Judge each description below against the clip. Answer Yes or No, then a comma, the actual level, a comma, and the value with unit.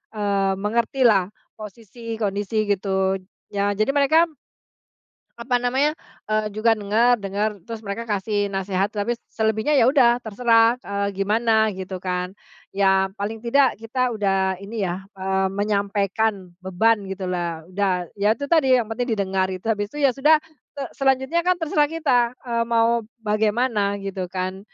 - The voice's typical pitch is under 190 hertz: No, high, 210 Hz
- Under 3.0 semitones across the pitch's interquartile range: No, average, 3.4 semitones